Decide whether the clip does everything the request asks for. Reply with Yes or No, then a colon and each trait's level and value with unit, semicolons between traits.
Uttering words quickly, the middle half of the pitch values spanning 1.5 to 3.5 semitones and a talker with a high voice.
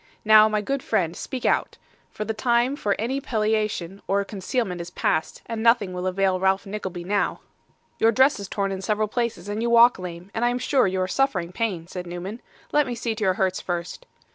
No: fast, 210 wpm; average, 4.0 semitones; high, 205 Hz